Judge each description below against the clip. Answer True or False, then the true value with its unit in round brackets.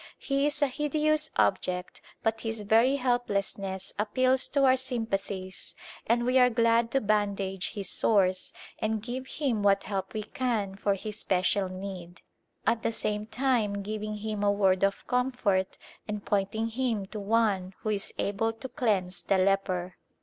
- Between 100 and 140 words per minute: False (165 wpm)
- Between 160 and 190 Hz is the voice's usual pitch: False (215 Hz)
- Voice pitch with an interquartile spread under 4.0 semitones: True (3.6 semitones)